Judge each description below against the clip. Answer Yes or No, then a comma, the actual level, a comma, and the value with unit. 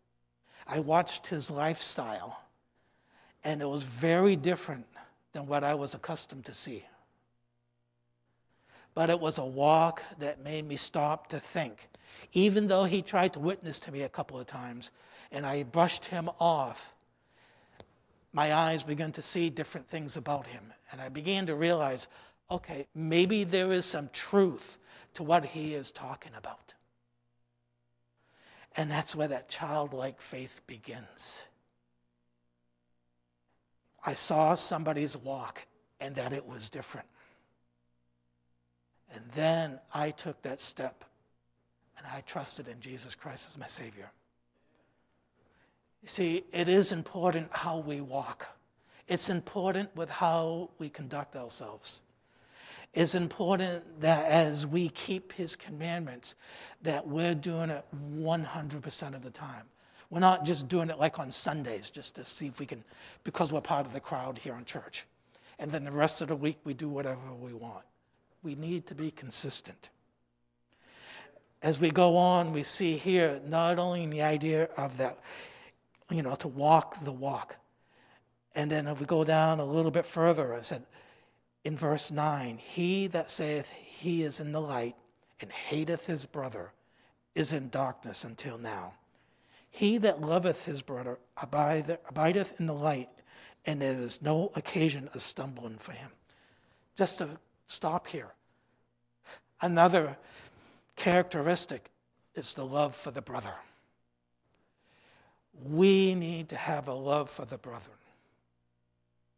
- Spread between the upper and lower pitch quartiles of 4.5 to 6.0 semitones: Yes, average, 5.1 semitones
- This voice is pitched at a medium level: Yes, medium, 150 Hz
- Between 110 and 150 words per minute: Yes, average, 145 wpm